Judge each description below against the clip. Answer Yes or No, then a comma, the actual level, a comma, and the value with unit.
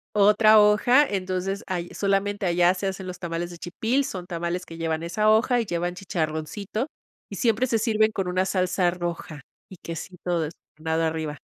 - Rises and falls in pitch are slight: No, average, 3.5 semitones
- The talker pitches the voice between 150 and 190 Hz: Yes, medium, 185 Hz